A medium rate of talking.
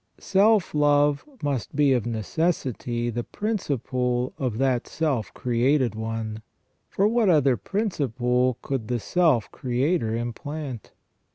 No: slow, 115 wpm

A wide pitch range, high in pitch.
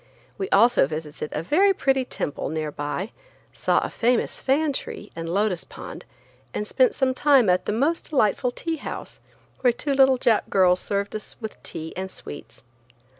Yes: wide, 6.8 semitones; high, 220 Hz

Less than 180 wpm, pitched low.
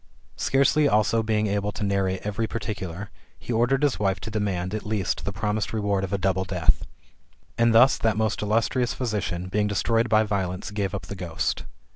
No: average, 185 wpm; low, 105 Hz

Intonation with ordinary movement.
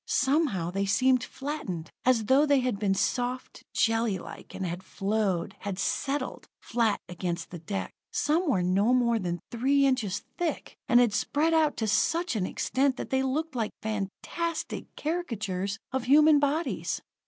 No: wide, 6.3 semitones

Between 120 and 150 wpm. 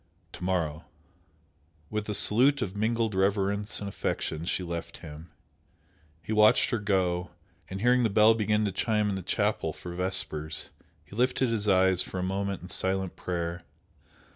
No: average, 165 wpm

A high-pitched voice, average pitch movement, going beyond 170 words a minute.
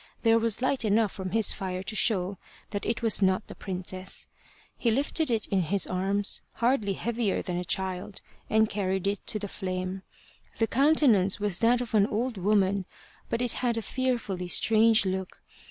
Yes: high, 205 Hz; average, 3.2 semitones; average, 180 wpm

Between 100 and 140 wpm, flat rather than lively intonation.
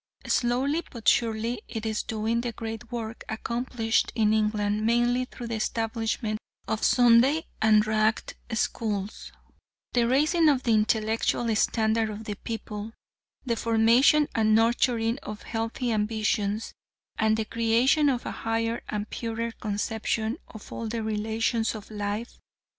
Yes: slow, 135 wpm; narrow, 1.6 semitones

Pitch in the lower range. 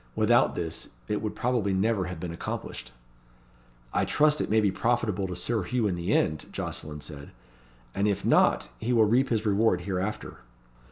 Yes: low, 100 Hz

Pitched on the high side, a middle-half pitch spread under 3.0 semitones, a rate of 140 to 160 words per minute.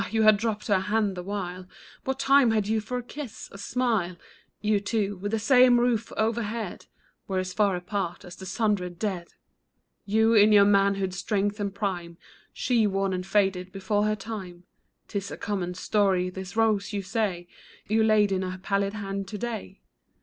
No: high, 205 Hz; narrow, 2.6 semitones; average, 180 wpm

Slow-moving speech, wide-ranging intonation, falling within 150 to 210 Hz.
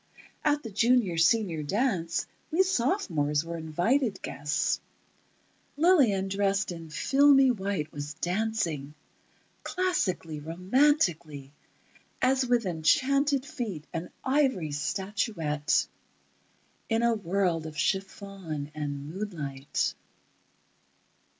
Yes: slow, 95 wpm; wide, 7.8 semitones; high, 190 Hz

